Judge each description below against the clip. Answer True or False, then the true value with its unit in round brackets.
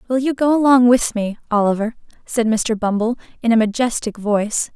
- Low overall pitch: False (230 Hz)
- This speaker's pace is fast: False (175 wpm)